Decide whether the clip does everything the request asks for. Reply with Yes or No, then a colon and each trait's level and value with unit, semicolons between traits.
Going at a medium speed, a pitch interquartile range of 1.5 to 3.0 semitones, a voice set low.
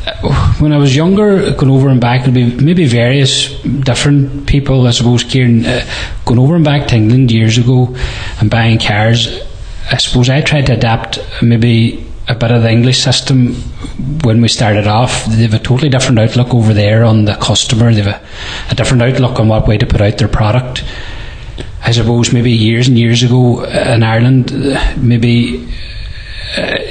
Yes: average, 180 wpm; narrow, 2.5 semitones; low, 120 Hz